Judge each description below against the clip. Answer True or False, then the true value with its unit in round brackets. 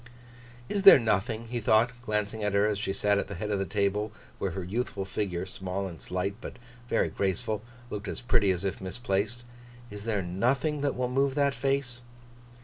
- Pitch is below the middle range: True (105 Hz)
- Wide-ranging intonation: False (3.7 semitones)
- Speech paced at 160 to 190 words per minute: False (200 wpm)